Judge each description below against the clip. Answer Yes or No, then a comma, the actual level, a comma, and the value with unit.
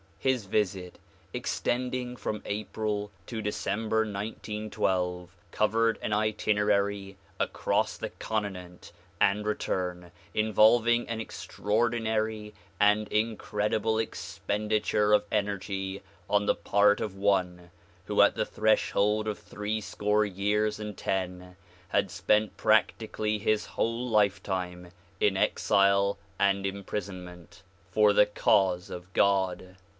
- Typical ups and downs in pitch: No, narrow, 1.8 semitones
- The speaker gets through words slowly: Yes, slow, 110 wpm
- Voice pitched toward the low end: Yes, low, 105 Hz